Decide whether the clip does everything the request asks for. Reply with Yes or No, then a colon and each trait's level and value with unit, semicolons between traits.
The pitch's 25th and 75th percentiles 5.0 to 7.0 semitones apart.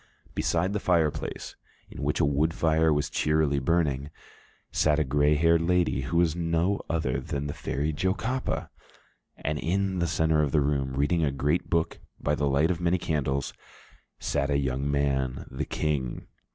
No: average, 3.0 semitones